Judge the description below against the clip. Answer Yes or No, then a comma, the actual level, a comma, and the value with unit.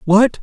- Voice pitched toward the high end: Yes, high, 210 Hz